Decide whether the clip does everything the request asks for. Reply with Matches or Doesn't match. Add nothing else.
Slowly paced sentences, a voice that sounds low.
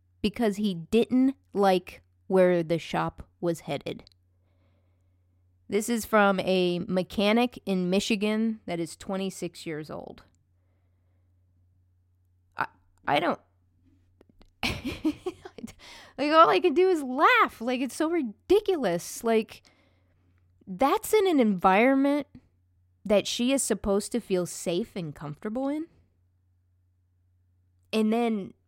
Doesn't match